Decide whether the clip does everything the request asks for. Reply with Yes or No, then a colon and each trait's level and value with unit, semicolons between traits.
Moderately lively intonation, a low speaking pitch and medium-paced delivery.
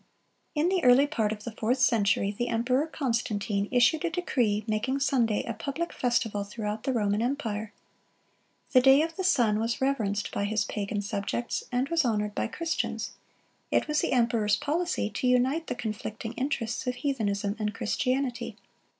No: average, 4.3 semitones; high, 235 Hz; average, 165 wpm